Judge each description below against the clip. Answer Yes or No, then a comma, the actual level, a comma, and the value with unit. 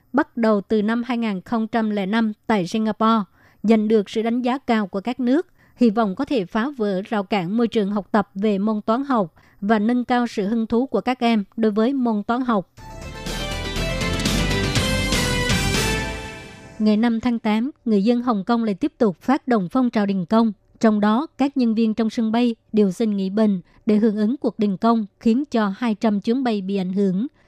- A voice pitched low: No, high, 225 Hz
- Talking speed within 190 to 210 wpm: Yes, average, 195 wpm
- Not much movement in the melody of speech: Yes, narrow, 2.1 semitones